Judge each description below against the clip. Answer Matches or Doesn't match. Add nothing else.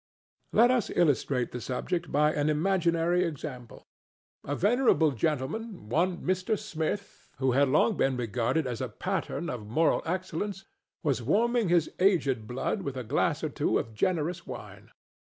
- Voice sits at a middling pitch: Matches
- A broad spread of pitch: Matches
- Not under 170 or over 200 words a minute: Doesn't match